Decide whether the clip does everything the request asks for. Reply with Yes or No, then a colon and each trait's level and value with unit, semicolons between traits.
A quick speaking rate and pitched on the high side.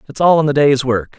No: fast, 305 wpm; medium, 140 Hz